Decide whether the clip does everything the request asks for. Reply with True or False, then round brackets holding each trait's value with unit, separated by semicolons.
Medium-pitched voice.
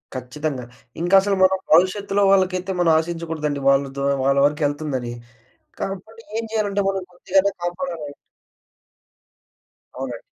True (175 Hz)